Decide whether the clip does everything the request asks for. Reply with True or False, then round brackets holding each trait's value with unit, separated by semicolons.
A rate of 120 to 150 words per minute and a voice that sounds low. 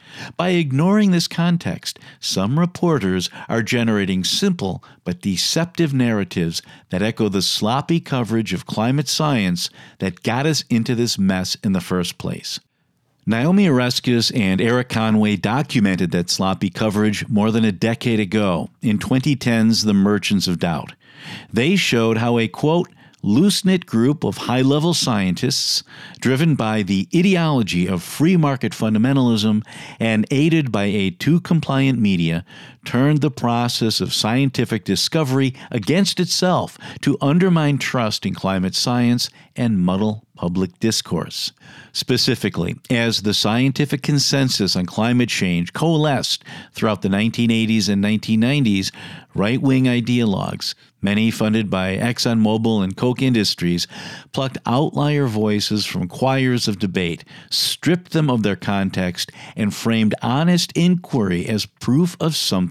True (135 wpm; 120 Hz)